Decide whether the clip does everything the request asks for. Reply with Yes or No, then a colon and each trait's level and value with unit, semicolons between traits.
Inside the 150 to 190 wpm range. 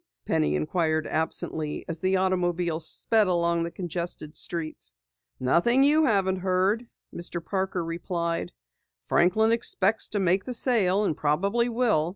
No: slow, 135 wpm